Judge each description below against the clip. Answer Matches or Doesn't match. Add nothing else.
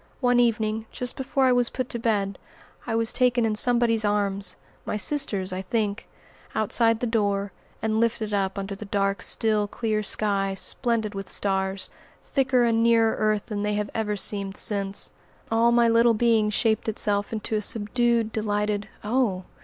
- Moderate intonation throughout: Doesn't match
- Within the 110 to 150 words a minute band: Doesn't match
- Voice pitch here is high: Matches